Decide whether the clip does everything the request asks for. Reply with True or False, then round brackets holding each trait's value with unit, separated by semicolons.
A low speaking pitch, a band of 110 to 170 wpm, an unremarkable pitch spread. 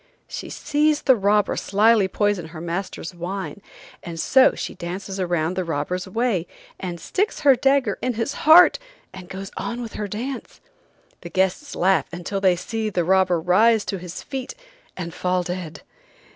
False (190 Hz; 165 wpm; 4.4 semitones)